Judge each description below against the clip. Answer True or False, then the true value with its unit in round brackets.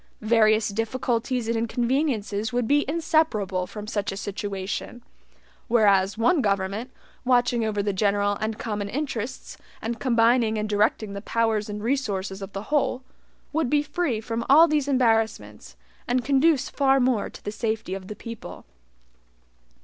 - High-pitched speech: True (225 Hz)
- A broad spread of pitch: False (3.7 semitones)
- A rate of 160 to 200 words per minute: False (150 wpm)